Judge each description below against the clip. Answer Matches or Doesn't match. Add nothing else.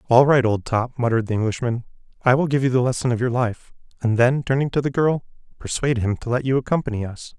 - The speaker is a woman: Doesn't match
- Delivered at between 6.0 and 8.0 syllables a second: Matches